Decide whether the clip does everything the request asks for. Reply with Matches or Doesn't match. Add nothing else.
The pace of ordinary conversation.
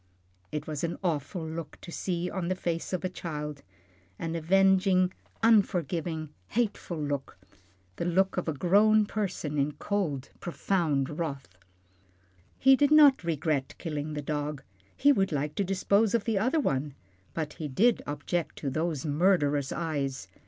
Matches